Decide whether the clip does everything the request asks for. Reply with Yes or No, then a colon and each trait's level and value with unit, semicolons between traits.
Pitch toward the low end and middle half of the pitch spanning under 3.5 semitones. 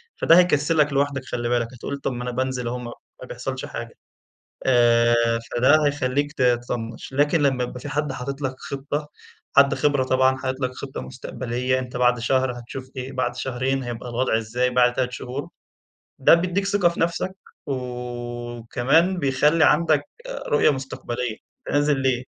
Yes: low, 130 Hz; average, 2.7 semitones